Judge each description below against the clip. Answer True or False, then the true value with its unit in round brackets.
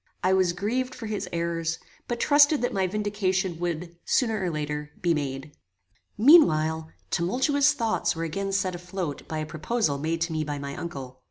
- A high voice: False (175 Hz)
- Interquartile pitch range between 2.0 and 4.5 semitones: False (5.1 semitones)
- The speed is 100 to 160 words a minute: False (175 wpm)